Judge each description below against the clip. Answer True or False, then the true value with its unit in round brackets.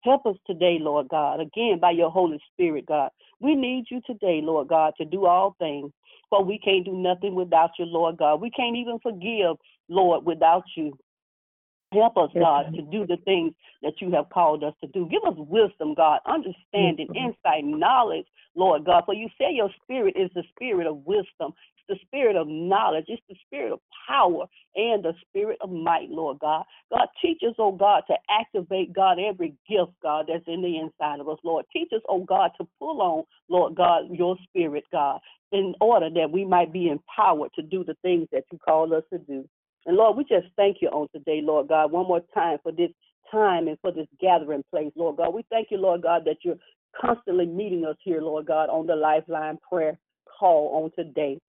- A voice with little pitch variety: False (4.1 semitones)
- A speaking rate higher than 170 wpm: True (205 wpm)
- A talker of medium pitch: True (175 Hz)